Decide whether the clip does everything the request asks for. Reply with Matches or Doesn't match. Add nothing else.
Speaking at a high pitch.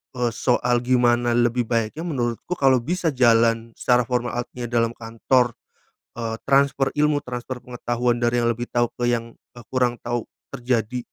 Doesn't match